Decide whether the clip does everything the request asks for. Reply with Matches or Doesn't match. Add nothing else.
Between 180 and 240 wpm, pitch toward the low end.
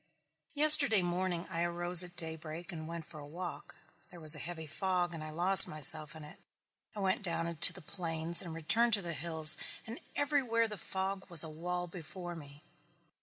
Doesn't match